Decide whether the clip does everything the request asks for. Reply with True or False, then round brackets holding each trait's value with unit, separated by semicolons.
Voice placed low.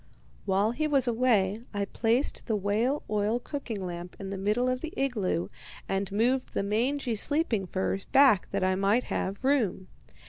False (215 Hz)